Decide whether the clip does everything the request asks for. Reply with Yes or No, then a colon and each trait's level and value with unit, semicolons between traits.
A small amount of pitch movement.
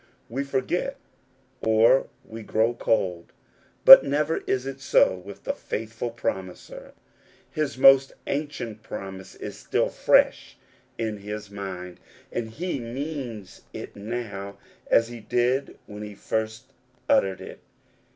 No: average, 4.4 semitones